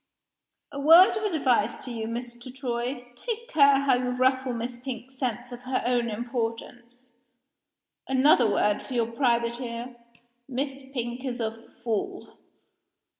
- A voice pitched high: Yes, high, 245 Hz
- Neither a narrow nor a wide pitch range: No, narrow, 2.0 semitones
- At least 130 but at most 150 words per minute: Yes, average, 140 wpm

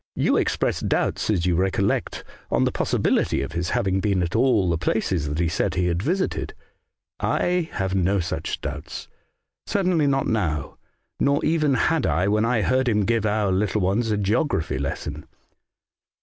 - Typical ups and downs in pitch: No, wide, 5.7 semitones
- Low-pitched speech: Yes, low, 100 Hz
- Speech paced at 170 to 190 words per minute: Yes, average, 175 wpm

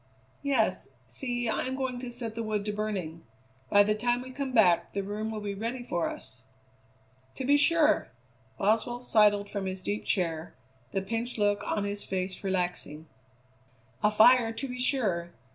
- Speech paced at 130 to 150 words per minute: No, average, 175 wpm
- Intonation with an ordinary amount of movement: Yes, average, 4.0 semitones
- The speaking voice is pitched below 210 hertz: No, high, 215 Hz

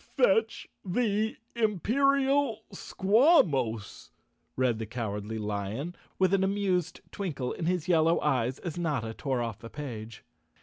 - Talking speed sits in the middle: No, slow, 125 wpm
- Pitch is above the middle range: No, medium, 165 Hz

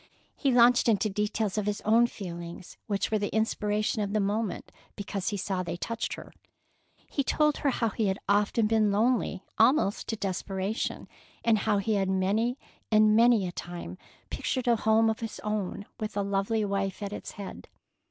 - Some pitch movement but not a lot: No, narrow, 2.2 semitones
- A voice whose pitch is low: No, high, 210 Hz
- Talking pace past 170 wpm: Yes, average, 180 wpm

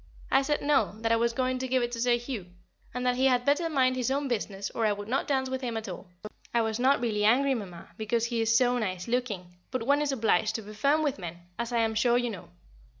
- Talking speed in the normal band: No, fast, 270 wpm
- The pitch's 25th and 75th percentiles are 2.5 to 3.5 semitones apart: Yes, average, 2.9 semitones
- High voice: Yes, high, 240 Hz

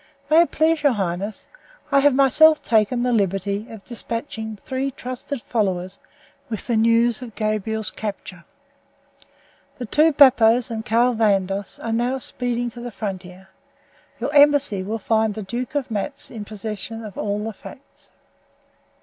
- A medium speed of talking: Yes, average, 150 wpm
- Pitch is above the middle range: Yes, high, 225 Hz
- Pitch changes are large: No, average, 3.4 semitones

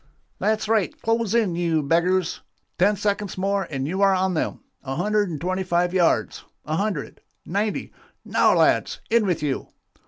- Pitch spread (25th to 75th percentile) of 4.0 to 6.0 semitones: No, average, 3.5 semitones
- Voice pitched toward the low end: No, medium, 185 Hz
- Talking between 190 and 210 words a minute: No, average, 165 wpm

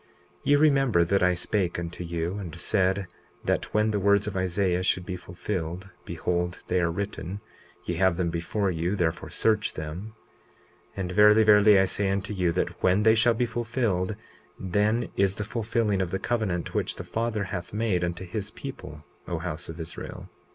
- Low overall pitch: Yes, very low, 95 Hz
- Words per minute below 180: No, average, 185 wpm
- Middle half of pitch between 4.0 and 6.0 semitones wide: No, average, 3.3 semitones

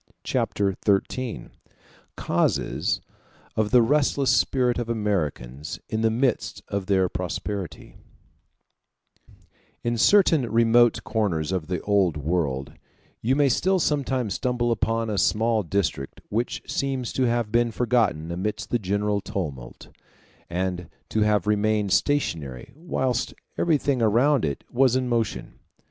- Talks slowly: Yes, slow, 125 wpm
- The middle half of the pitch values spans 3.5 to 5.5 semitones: Yes, average, 4.7 semitones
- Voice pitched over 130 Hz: No, low, 110 Hz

